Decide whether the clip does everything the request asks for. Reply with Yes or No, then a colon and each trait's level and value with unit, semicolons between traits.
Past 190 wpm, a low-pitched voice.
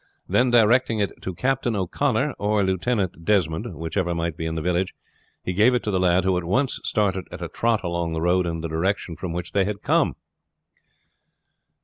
Yes: average, 200 wpm; very low, 95 Hz